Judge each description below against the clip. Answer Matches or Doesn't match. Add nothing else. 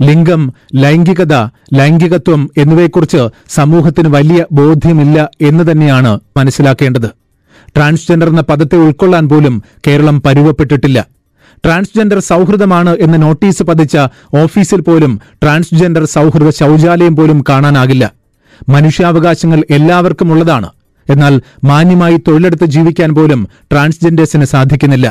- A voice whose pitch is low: Doesn't match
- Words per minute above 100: Doesn't match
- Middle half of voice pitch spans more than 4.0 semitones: Doesn't match